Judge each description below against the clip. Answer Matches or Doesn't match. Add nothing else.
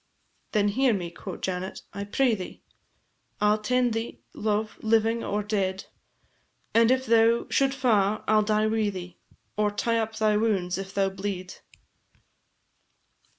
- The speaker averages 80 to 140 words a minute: Doesn't match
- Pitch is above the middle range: Matches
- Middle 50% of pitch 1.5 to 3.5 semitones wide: Matches